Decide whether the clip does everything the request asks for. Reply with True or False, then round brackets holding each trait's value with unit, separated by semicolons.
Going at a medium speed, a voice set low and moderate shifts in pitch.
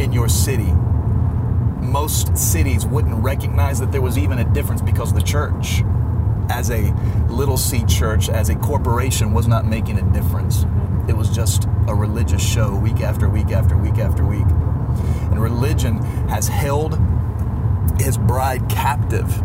False (150 wpm; 105 Hz; 1.9 semitones)